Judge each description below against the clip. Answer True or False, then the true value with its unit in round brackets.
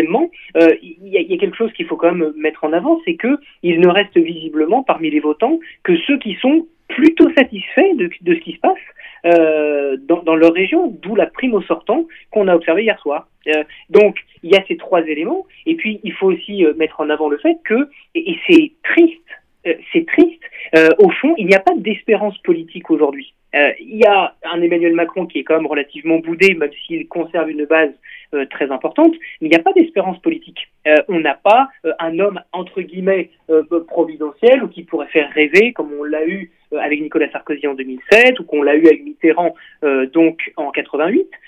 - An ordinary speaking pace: False (220 wpm)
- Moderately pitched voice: True (175 Hz)